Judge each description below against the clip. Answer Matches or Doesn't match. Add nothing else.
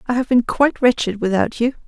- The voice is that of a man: Doesn't match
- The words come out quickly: Matches